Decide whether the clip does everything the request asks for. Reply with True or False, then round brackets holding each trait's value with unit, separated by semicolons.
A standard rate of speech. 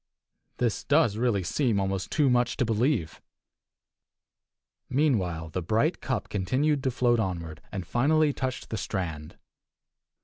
False (130 wpm)